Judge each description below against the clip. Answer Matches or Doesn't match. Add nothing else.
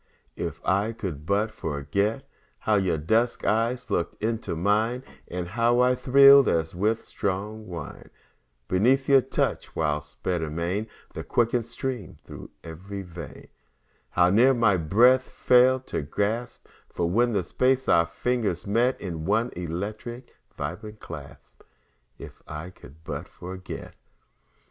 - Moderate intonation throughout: Doesn't match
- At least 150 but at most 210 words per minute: Doesn't match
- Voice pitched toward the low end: Matches